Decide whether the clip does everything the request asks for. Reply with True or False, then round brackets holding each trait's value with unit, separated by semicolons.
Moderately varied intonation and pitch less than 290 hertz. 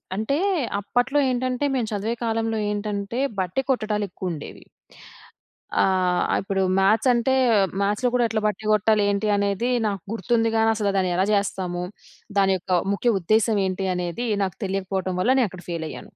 True (3.1 semitones; 205 Hz)